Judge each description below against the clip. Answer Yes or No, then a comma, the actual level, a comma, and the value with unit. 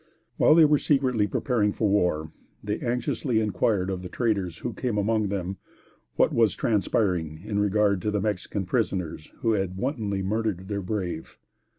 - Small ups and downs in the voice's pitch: No, average, 3.2 semitones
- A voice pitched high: No, low, 105 Hz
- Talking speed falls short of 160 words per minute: No, average, 165 wpm